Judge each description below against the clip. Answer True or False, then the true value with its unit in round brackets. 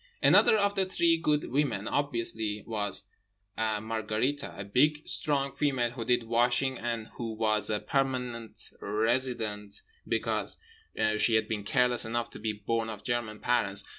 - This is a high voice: False (115 Hz)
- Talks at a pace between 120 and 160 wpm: True (140 wpm)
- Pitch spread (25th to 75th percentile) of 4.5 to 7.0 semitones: False (3.5 semitones)